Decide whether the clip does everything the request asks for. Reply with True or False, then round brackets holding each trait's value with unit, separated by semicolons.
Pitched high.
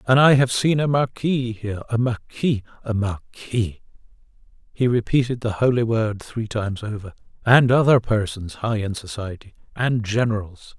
False (115 Hz)